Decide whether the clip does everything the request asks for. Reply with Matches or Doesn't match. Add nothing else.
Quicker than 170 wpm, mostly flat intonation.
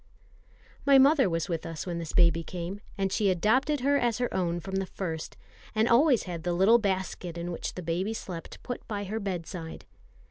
Doesn't match